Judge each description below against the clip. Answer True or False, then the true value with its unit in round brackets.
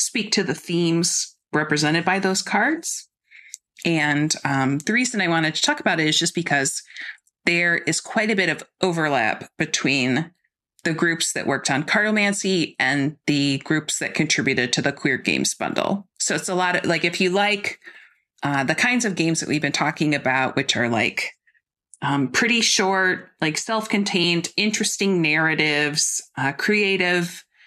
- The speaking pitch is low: False (170 Hz)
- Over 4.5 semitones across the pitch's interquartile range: True (4.9 semitones)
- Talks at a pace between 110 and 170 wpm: True (165 wpm)